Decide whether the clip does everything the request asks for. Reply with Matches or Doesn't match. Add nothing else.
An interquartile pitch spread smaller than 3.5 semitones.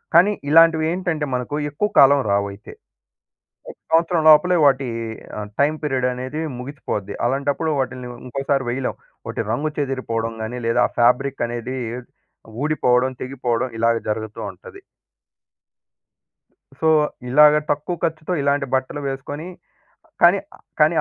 Doesn't match